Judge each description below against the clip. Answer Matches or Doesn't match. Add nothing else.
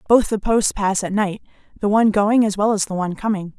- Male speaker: Doesn't match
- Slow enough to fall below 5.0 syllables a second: Doesn't match